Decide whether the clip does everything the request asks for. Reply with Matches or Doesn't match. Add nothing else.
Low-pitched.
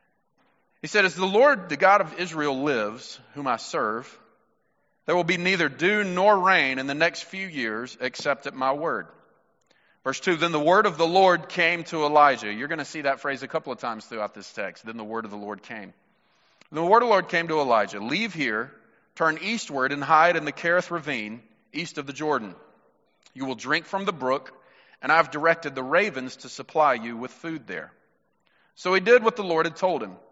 Doesn't match